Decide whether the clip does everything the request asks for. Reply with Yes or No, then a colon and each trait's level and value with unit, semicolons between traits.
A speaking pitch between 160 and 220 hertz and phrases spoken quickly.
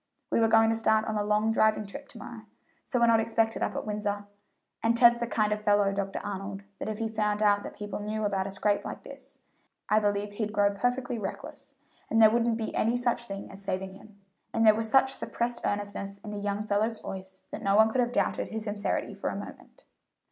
Yes: high, 215 Hz; fast, 230 wpm